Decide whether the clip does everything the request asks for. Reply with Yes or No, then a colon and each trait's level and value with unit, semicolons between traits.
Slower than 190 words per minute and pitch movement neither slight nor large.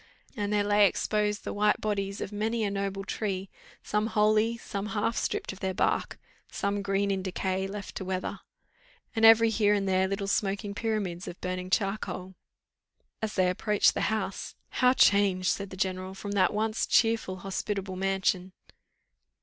No: average, 170 wpm; narrow, 1.9 semitones